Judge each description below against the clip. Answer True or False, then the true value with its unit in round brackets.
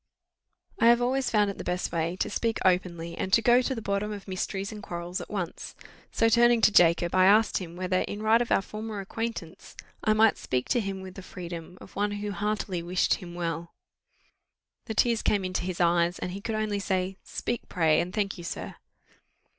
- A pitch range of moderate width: True (3.4 semitones)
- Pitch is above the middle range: True (195 Hz)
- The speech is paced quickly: True (210 wpm)